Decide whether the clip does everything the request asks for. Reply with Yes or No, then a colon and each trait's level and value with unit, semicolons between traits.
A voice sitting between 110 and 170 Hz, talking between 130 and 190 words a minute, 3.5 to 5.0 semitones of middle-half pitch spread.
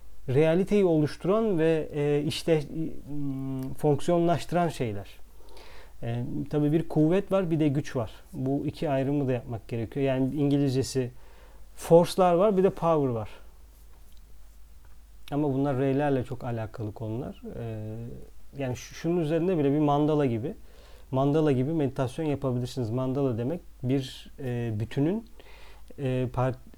No: low, 135 Hz; average, 110 wpm; average, 4.3 semitones